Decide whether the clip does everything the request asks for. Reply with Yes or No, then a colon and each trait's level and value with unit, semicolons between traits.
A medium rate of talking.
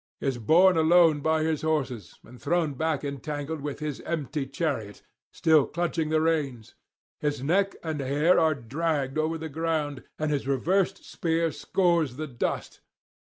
Yes: average, 155 wpm